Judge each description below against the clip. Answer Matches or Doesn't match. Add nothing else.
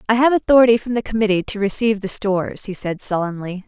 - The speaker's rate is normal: Doesn't match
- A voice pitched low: Doesn't match